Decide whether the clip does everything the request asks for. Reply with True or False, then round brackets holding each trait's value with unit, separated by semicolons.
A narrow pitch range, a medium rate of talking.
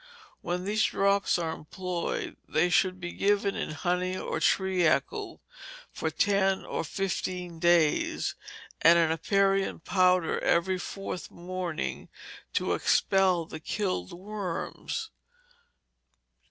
False (2.3 semitones; 110 wpm)